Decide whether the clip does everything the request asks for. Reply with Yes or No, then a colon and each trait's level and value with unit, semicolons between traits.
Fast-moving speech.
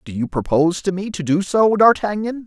Yes: fast, 220 wpm